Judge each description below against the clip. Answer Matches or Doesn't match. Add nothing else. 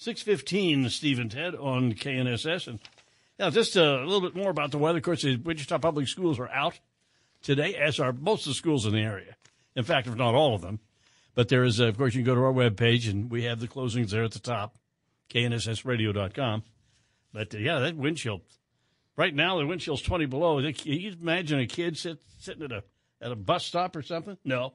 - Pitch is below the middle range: Matches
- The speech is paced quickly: Matches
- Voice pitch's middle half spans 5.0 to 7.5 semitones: Matches